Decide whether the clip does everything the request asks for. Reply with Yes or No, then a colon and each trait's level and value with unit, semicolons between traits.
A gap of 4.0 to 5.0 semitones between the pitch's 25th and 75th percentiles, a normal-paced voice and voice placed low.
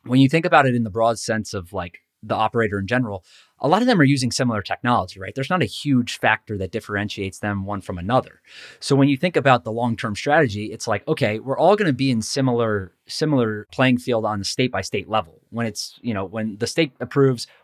No: average, 4.3 semitones; fast, 240 wpm; low, 115 Hz